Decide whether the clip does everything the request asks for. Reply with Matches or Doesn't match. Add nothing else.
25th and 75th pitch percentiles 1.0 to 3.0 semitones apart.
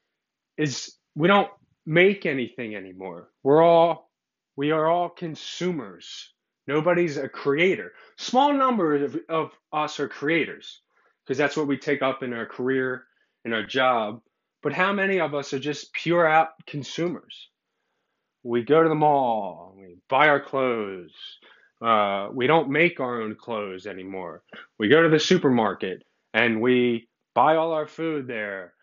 Doesn't match